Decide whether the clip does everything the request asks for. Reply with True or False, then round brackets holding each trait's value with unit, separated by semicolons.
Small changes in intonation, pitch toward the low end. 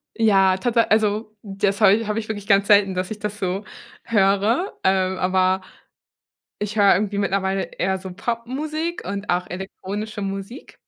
False (2.1 semitones; 200 Hz)